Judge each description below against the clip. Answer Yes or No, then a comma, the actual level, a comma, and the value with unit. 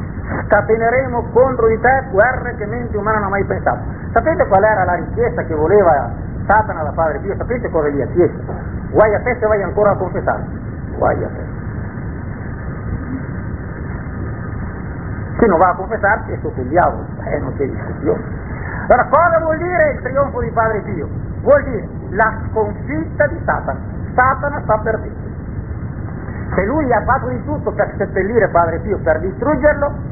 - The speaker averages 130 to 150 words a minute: No, average, 165 wpm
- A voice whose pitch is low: No, high, 215 Hz